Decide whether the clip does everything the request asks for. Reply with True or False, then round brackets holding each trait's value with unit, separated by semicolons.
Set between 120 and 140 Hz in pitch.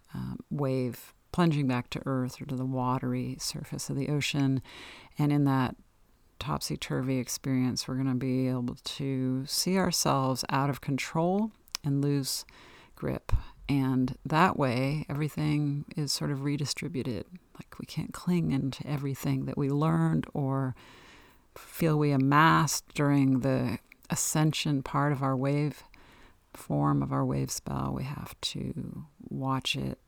True (135 Hz)